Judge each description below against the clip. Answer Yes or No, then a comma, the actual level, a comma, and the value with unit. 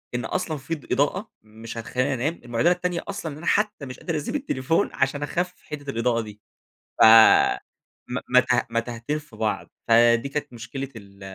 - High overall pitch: No, low, 135 Hz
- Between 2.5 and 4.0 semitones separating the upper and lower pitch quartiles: No, wide, 5.6 semitones